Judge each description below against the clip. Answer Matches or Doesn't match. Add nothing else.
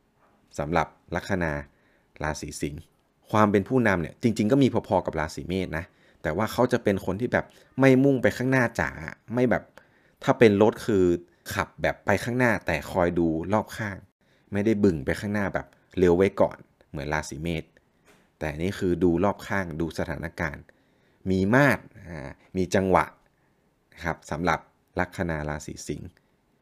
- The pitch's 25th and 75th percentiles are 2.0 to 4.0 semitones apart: Doesn't match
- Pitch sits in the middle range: Doesn't match